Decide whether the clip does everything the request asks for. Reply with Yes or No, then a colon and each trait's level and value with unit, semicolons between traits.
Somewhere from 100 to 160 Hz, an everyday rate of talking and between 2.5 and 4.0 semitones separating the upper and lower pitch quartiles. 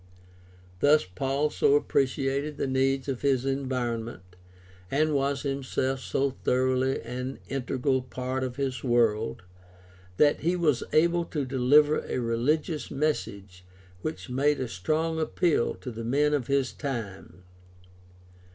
No: low, 135 Hz; slow, 130 wpm; average, 2.8 semitones